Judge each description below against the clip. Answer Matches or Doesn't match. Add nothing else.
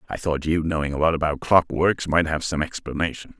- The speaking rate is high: Matches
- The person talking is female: Doesn't match